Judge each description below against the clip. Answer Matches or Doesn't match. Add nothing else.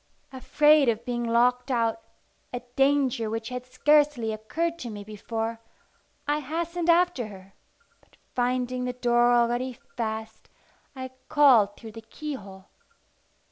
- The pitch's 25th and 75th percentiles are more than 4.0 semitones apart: Doesn't match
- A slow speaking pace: Matches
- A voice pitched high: Matches